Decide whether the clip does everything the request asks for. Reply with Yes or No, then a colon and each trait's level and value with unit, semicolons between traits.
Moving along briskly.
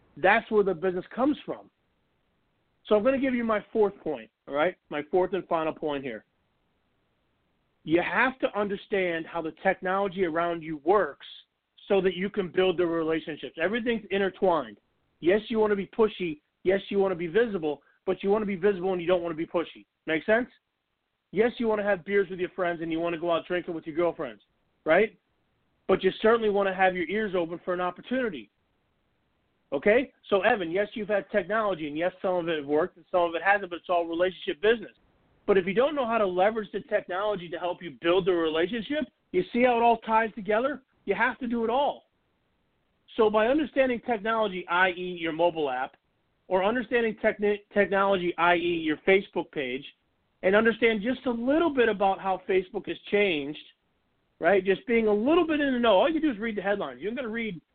Yes: fast, 210 wpm